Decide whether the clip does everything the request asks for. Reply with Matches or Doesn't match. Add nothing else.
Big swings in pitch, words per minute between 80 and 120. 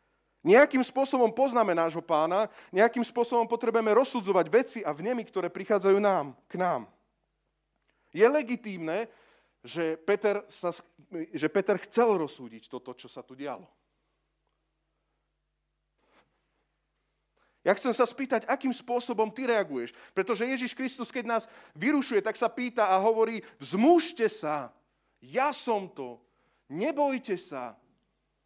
Matches